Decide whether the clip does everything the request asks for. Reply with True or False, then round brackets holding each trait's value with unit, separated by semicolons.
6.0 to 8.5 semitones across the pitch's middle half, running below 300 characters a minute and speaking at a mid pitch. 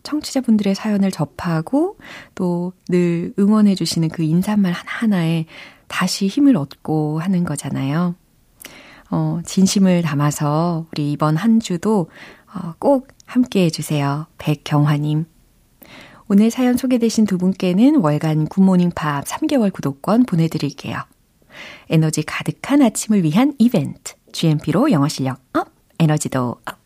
False (5.4 semitones; 275 characters per minute; 175 Hz)